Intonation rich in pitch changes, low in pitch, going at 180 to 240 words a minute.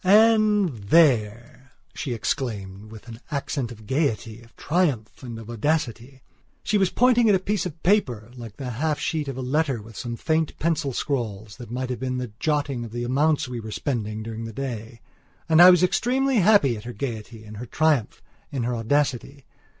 Yes: wide, 5.7 semitones; low, 130 Hz; average, 190 wpm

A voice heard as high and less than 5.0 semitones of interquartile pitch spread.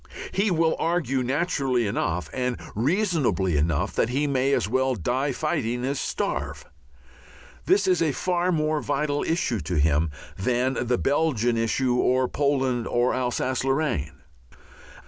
No: low, 130 Hz; average, 4.5 semitones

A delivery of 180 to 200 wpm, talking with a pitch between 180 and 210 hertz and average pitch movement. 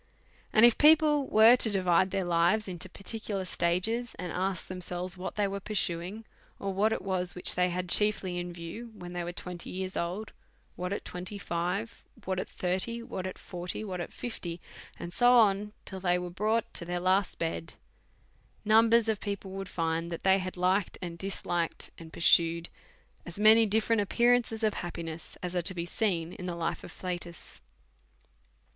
Yes: average, 185 wpm; medium, 185 Hz; average, 3.4 semitones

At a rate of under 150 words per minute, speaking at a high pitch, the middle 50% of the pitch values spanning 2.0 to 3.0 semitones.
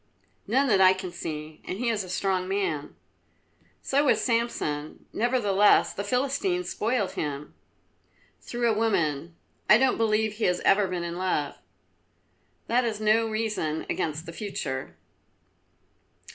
No: average, 140 wpm; high, 200 Hz; average, 5.1 semitones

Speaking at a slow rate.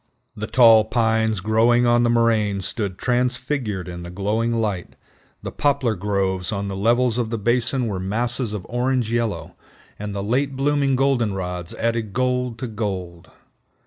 No: average, 155 wpm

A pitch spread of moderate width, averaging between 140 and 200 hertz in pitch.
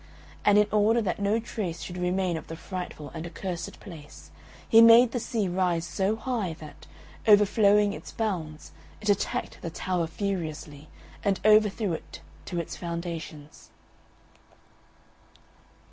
Yes: average, 3.9 semitones; medium, 185 Hz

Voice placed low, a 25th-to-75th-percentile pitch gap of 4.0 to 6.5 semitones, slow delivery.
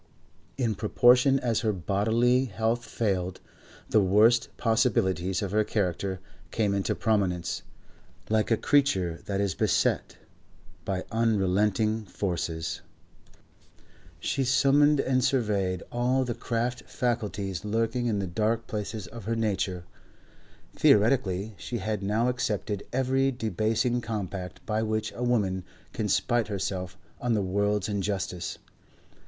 No: low, 110 Hz; average, 3.6 semitones; slow, 125 wpm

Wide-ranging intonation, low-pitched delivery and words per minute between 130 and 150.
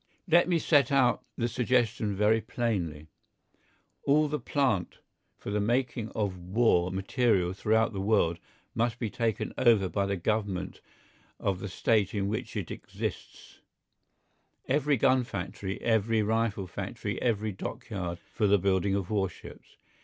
No: average, 3.6 semitones; low, 110 Hz; average, 140 wpm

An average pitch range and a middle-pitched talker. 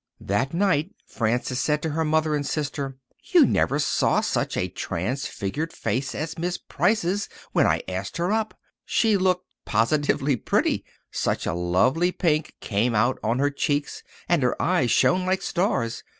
No: wide, 6.3 semitones; medium, 145 Hz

